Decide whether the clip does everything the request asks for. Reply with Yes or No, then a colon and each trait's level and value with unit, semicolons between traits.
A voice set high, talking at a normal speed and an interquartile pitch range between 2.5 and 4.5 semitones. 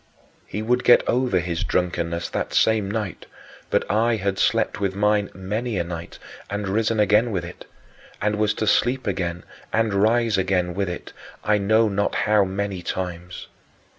No: low, 100 Hz; average, 165 wpm; average, 2.9 semitones